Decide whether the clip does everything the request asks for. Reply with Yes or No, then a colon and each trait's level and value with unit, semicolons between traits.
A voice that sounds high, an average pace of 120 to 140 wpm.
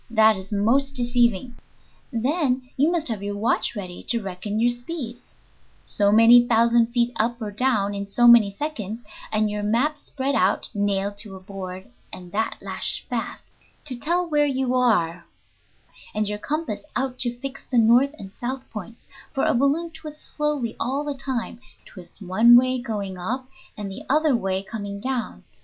No: high, 235 Hz; average, 175 wpm